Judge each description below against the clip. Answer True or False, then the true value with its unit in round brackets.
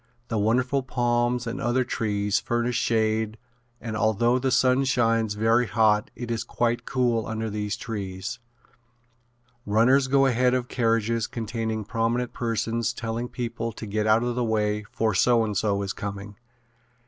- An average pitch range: False (2.1 semitones)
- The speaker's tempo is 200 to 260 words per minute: False (155 wpm)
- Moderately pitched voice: False (115 Hz)